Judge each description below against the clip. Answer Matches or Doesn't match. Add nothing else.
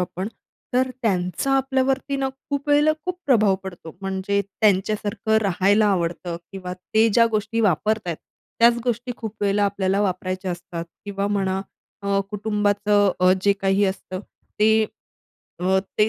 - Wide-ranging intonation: Doesn't match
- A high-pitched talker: Matches